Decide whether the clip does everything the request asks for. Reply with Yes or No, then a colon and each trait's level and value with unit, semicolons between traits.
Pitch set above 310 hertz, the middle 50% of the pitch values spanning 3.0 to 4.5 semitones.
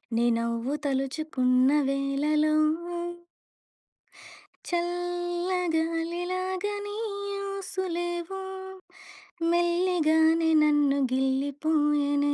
Yes: very high, 320 Hz; average, 3.6 semitones